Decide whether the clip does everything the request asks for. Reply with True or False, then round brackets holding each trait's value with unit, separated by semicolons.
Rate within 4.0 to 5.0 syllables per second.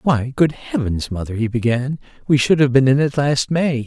True (4.9 syllables/s)